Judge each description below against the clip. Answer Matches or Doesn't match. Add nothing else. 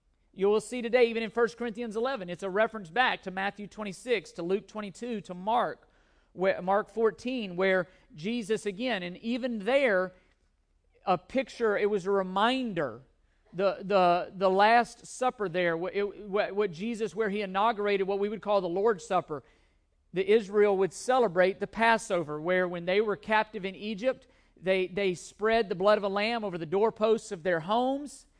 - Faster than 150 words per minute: Matches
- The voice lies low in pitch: Doesn't match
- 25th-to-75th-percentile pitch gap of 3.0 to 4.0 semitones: Matches